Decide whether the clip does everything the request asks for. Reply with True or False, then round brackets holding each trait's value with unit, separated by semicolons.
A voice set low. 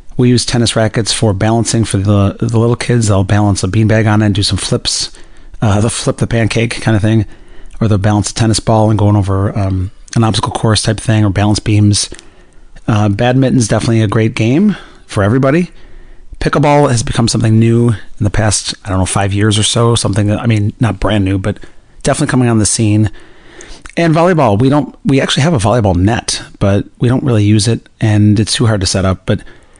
True (110 Hz)